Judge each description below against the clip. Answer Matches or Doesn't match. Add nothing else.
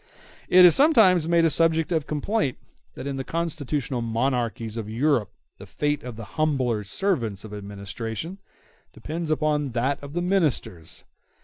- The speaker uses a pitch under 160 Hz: Matches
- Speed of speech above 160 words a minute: Doesn't match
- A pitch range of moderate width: Doesn't match